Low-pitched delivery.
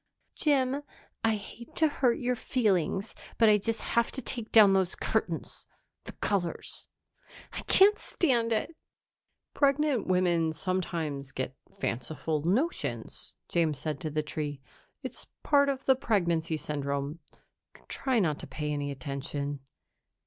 No: medium, 185 Hz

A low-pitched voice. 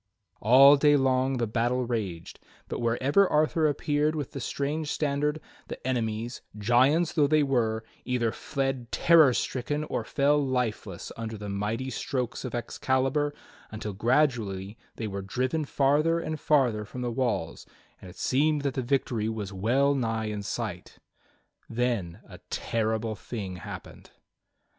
Yes: low, 125 Hz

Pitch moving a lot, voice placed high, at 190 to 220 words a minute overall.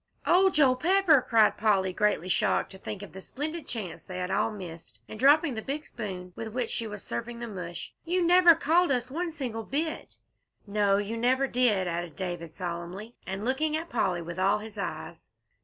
Yes: wide, 6.8 semitones; high, 220 Hz; average, 195 wpm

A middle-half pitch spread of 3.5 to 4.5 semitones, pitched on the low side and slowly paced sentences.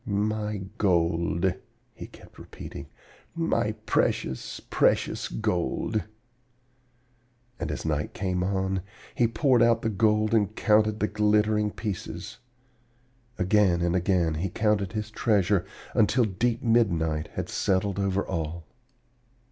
No: average, 3.1 semitones; low, 100 Hz; slow, 115 wpm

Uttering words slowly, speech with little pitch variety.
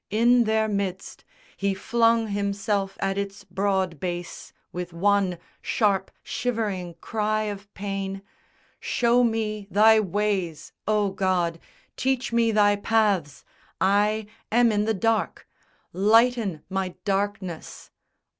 Yes: slow, 115 wpm; narrow, 2.3 semitones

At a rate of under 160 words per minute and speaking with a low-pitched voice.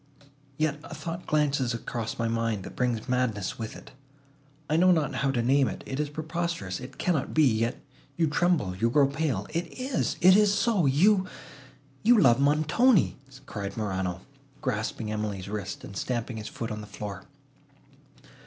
Yes: average, 150 wpm; low, 130 Hz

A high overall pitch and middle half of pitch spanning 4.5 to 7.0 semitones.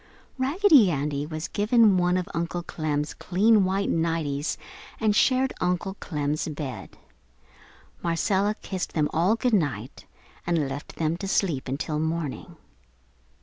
No: medium, 170 Hz; average, 4.9 semitones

